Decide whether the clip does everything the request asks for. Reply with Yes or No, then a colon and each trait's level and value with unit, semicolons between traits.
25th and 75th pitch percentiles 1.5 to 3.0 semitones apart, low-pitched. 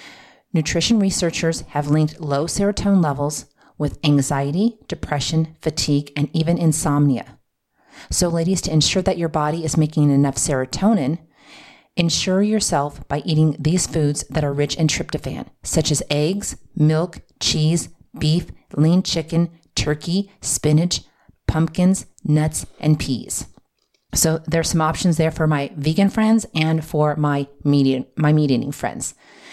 No: narrow, 2.6 semitones; medium, 155 Hz